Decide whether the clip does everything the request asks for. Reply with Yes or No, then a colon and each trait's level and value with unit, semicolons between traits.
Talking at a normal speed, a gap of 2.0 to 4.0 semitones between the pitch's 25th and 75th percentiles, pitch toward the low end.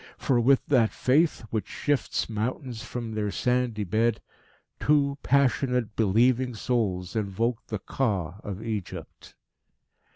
No: slow, 120 wpm; average, 3.2 semitones; low, 115 Hz